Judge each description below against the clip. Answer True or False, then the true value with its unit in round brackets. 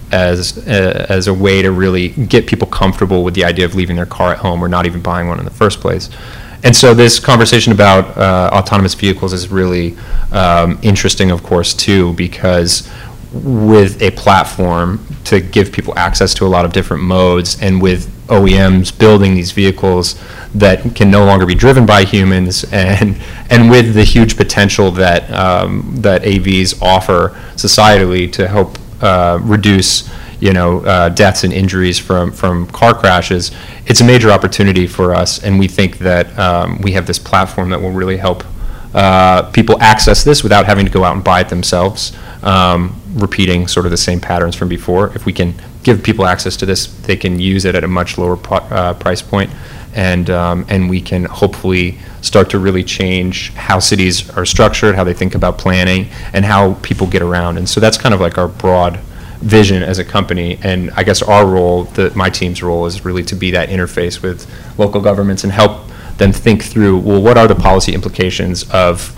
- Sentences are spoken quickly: False (195 wpm)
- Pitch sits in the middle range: False (95 Hz)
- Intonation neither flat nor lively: False (2.3 semitones)